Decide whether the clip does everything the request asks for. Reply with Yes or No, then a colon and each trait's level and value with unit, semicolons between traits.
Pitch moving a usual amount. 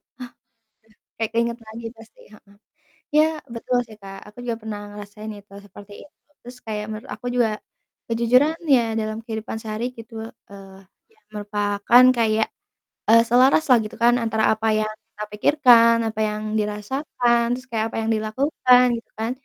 No: narrow, 2.2 semitones